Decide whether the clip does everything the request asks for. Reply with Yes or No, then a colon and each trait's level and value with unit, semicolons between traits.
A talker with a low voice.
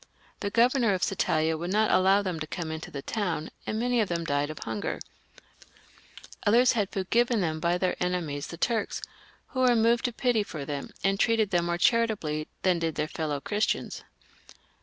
No: medium, 185 Hz